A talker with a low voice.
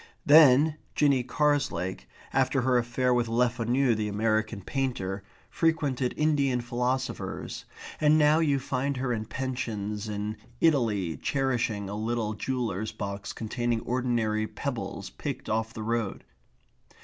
Yes: low, 120 Hz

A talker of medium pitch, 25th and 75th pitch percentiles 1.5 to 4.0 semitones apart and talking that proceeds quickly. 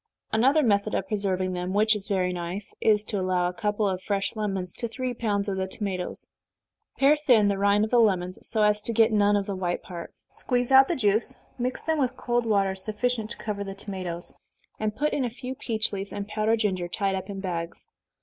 No: high, 205 Hz; average, 3.1 semitones; fast, 220 wpm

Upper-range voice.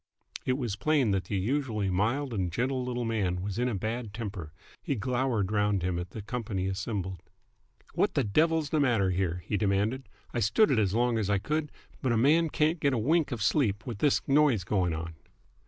No: low, 110 Hz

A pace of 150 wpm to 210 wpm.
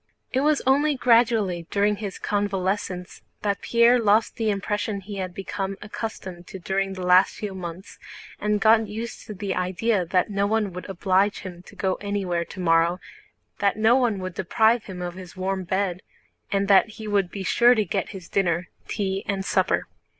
Yes: average, 180 wpm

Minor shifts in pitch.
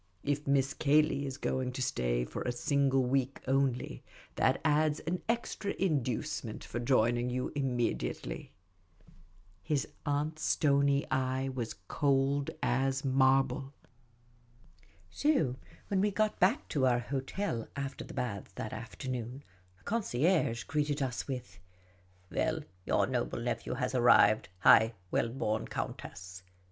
No: average, 3.1 semitones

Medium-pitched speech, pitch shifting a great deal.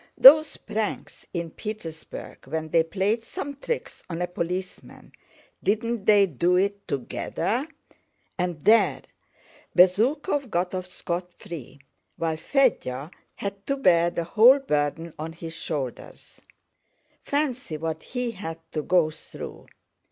Yes: medium, 180 Hz; wide, 5.8 semitones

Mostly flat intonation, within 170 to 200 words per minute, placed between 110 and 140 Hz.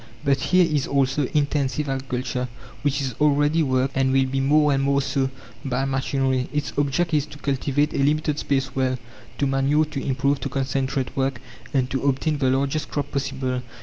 Yes: narrow, 1.7 semitones; average, 180 wpm; low, 135 Hz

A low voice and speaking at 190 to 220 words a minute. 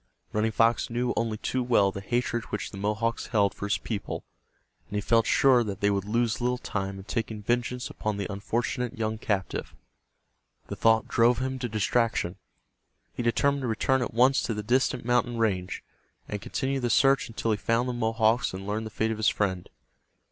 Yes: low, 115 Hz; average, 195 wpm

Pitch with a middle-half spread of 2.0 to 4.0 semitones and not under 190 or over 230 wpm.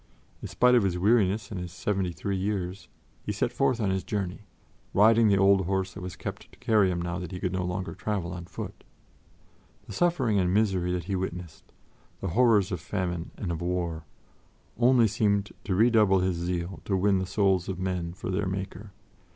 Yes: narrow, 2.4 semitones; average, 200 wpm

